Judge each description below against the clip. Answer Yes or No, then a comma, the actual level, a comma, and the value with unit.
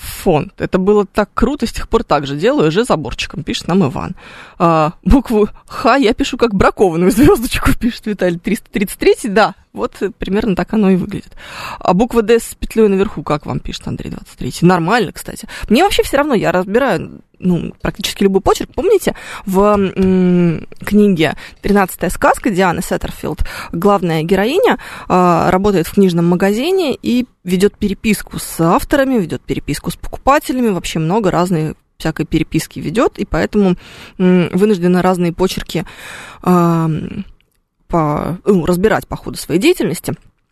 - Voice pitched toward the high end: Yes, high, 195 Hz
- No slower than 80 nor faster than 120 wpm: No, average, 150 wpm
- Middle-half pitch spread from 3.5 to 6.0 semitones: Yes, average, 4.1 semitones